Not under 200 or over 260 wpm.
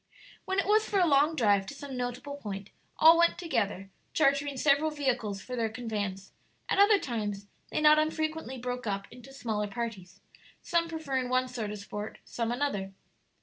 No: average, 175 wpm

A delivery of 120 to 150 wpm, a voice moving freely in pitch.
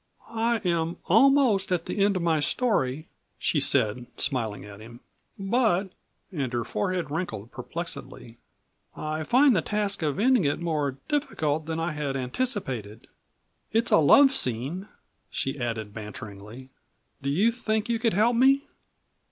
Yes: average, 145 wpm; wide, 9.0 semitones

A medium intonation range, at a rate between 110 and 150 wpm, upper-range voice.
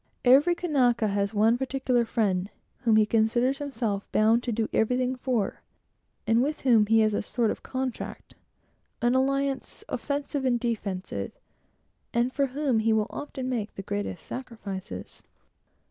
Yes: average, 3.4 semitones; average, 145 wpm; high, 235 Hz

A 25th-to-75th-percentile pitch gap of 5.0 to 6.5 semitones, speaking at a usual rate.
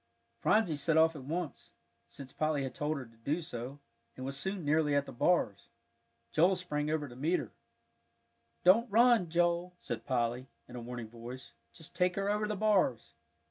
Yes: wide, 5.6 semitones; average, 180 wpm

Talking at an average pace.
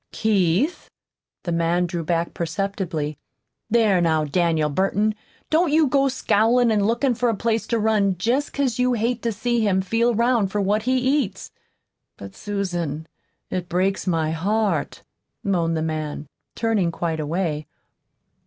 Yes: average, 155 wpm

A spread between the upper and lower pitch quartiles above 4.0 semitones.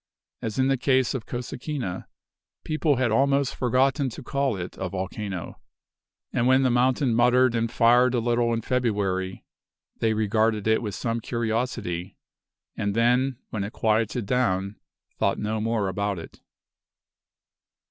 No: average, 3.3 semitones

